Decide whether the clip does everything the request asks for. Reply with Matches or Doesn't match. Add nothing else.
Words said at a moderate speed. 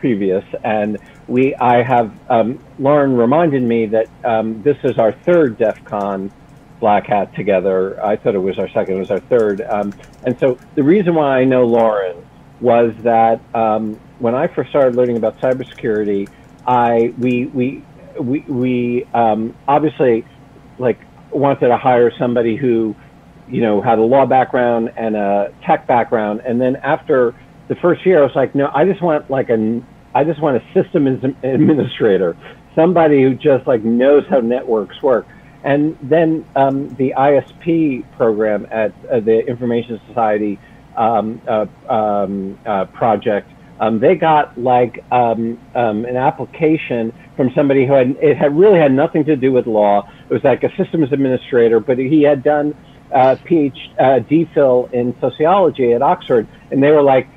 Matches